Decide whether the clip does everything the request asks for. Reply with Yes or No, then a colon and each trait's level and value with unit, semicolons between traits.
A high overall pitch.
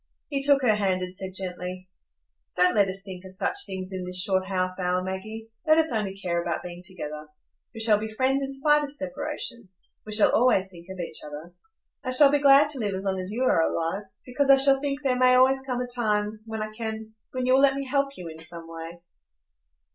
Yes: high, 215 Hz